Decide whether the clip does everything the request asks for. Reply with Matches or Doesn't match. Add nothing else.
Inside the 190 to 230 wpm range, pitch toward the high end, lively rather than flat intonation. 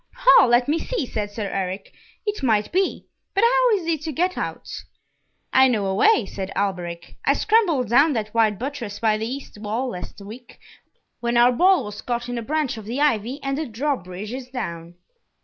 Matches